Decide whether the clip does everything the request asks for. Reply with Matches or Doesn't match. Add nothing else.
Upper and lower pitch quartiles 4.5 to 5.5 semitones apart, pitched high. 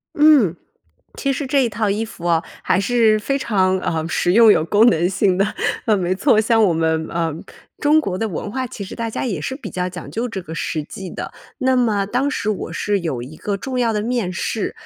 Matches